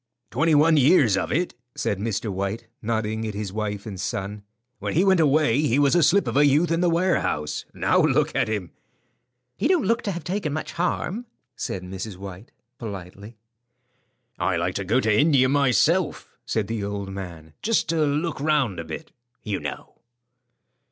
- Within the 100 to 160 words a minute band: No, average, 180 wpm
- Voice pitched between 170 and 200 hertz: No, low, 115 Hz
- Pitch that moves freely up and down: Yes, wide, 7.9 semitones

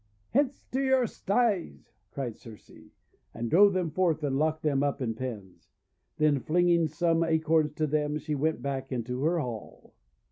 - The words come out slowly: No, average, 170 wpm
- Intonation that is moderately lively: Yes, average, 4.3 semitones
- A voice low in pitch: No, medium, 155 Hz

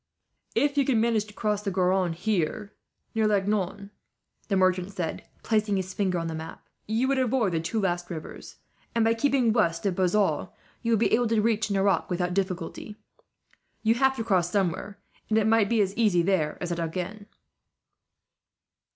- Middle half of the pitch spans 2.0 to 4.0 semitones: Yes, average, 3.6 semitones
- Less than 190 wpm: Yes, average, 180 wpm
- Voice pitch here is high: Yes, high, 200 Hz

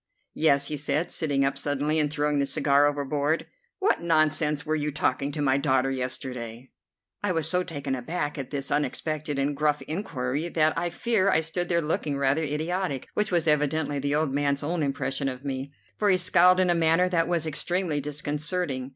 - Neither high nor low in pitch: Yes, medium, 150 Hz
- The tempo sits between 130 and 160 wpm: No, average, 190 wpm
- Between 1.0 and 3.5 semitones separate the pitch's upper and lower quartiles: Yes, average, 2.9 semitones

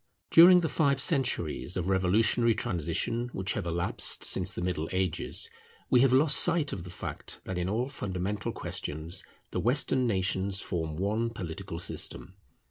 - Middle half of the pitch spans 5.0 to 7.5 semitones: Yes, wide, 5.5 semitones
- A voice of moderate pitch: No, very low, 95 Hz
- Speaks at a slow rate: No, average, 155 wpm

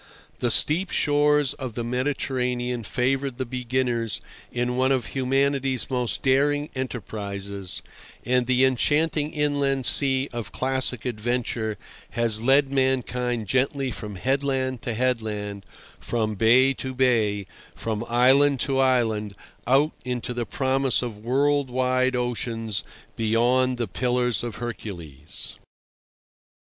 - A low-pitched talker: Yes, low, 125 Hz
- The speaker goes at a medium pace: No, slow, 120 wpm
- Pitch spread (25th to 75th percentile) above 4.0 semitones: No, narrow, 2.4 semitones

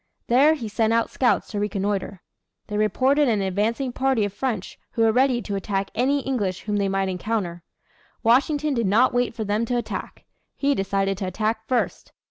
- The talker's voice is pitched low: No, high, 220 Hz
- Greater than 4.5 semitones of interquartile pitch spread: No, average, 4.2 semitones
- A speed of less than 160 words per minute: No, average, 185 wpm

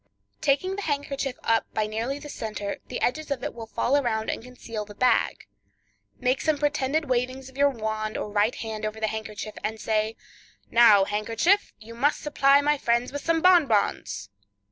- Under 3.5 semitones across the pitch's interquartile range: No, average, 4.5 semitones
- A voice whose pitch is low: No, high, 240 Hz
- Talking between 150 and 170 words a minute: No, average, 180 wpm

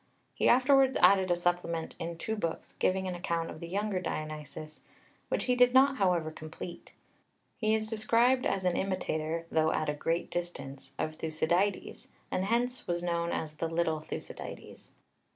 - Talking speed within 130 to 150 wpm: No, average, 165 wpm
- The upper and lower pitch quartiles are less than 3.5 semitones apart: No, average, 4.8 semitones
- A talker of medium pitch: Yes, medium, 175 Hz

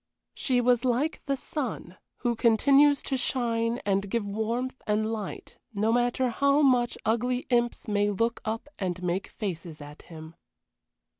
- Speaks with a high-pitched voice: Yes, high, 230 Hz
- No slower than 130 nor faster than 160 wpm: Yes, average, 150 wpm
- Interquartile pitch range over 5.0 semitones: No, average, 3.5 semitones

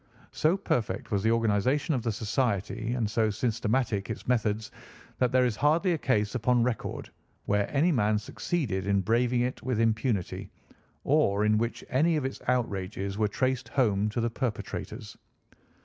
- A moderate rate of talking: Yes, average, 165 wpm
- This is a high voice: No, low, 115 Hz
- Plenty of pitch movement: No, average, 3.6 semitones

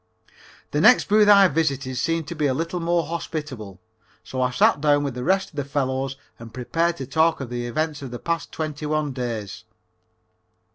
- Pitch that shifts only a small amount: No, average, 4.2 semitones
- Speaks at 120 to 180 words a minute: No, average, 195 wpm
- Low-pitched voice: No, medium, 145 Hz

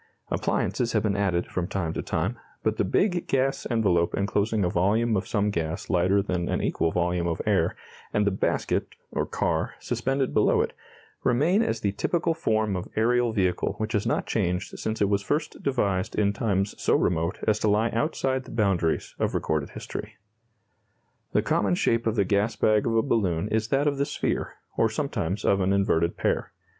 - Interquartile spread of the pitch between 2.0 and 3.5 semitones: No, average, 3.9 semitones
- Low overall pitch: Yes, low, 105 Hz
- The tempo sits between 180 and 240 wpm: Yes, average, 190 wpm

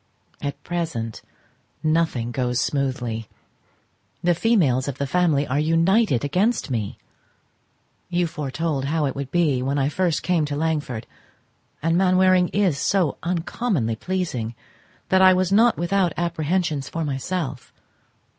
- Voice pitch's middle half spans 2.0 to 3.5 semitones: No, average, 4.9 semitones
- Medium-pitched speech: Yes, medium, 160 Hz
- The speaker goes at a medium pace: No, slow, 130 wpm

